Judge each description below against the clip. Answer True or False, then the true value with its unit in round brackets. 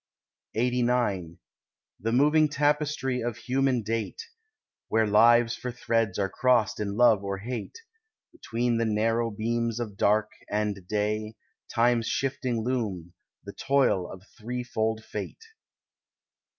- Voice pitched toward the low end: True (115 Hz)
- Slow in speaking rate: True (120 wpm)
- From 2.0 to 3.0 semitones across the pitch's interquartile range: True (2.7 semitones)